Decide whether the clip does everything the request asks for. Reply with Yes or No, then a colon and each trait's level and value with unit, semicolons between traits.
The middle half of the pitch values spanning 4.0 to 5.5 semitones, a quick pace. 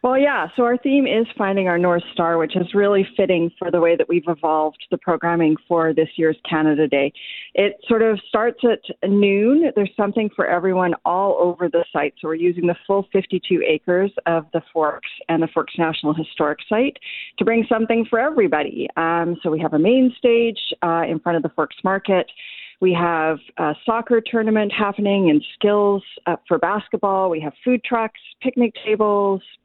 No: average, 4.5 semitones; average, 190 wpm